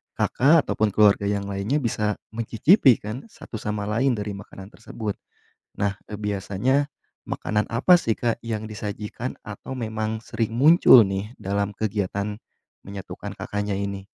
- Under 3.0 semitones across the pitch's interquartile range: Yes, narrow, 2.4 semitones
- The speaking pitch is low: Yes, low, 105 Hz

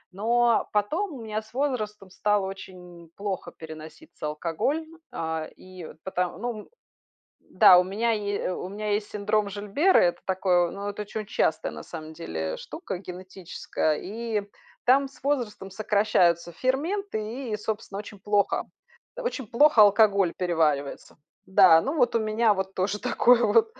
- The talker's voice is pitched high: Yes, high, 205 Hz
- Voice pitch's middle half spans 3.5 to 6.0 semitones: Yes, average, 4.1 semitones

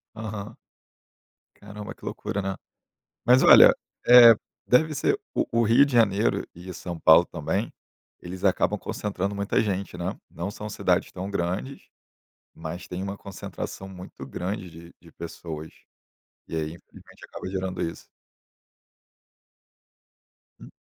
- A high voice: No, very low, 95 Hz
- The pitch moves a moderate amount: Yes, average, 3.3 semitones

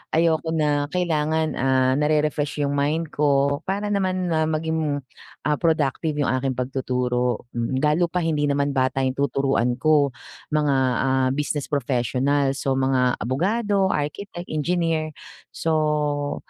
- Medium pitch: Yes, medium, 145 Hz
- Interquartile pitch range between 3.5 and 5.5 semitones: No, average, 3.0 semitones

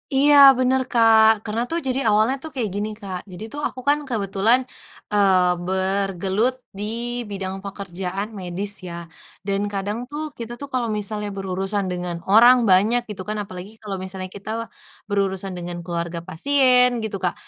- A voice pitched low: No, high, 200 Hz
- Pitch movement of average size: Yes, average, 3.6 semitones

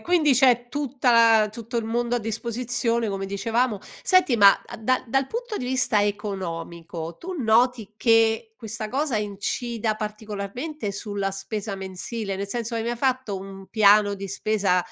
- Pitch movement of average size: Yes, average, 3.5 semitones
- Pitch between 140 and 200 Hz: No, high, 220 Hz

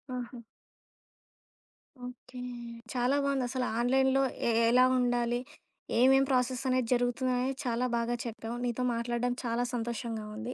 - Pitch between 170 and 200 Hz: No, high, 245 Hz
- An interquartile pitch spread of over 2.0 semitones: No, narrow, 1.3 semitones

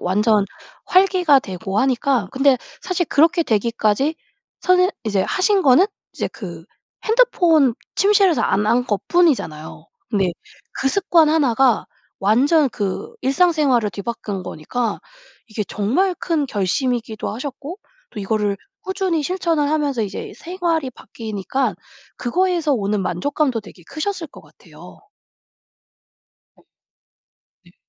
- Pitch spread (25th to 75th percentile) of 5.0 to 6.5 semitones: No, wide, 8.0 semitones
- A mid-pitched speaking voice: No, very high, 270 Hz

